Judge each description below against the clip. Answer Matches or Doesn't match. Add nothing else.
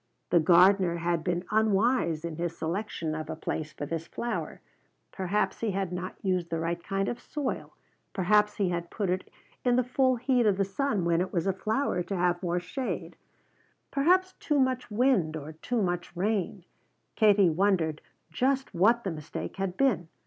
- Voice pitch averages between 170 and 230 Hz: Matches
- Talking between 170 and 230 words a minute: Matches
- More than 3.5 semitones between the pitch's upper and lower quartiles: Matches